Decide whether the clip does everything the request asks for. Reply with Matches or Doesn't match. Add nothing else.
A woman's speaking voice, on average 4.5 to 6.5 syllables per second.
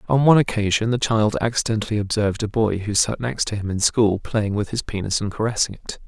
Doesn't match